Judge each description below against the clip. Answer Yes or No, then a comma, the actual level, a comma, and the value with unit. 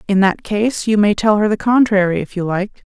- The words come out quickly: Yes, fast, 250 wpm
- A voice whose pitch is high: Yes, high, 205 Hz